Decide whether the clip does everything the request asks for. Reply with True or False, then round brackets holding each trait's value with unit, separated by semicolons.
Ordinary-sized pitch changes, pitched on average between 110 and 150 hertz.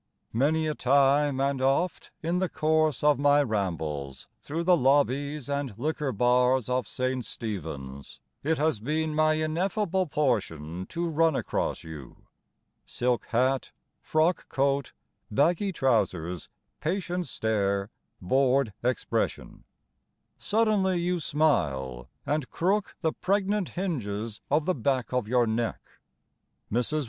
False (5.9 semitones; 140 Hz)